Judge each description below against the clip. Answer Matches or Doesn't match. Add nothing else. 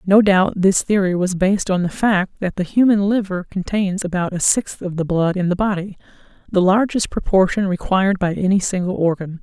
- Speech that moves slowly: Doesn't match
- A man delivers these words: Doesn't match